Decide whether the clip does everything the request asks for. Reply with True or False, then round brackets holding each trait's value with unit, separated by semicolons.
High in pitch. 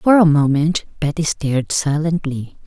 False (155 Hz)